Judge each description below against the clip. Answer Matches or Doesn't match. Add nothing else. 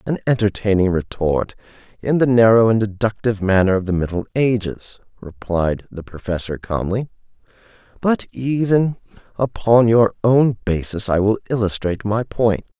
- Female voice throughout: Doesn't match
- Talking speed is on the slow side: Matches